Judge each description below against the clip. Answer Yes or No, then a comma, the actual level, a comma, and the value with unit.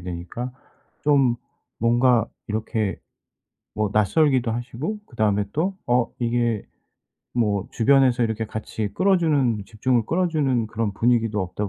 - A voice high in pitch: No, low, 115 Hz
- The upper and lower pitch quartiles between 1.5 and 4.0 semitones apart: Yes, average, 3.4 semitones